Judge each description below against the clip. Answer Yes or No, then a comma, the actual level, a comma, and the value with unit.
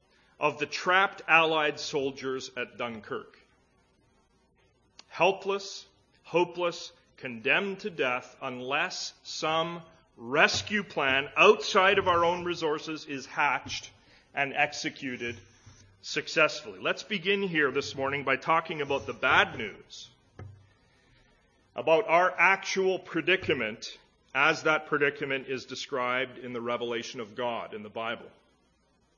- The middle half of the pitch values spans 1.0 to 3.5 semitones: No, average, 5.2 semitones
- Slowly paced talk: Yes, slow, 110 wpm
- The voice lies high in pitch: No, medium, 150 Hz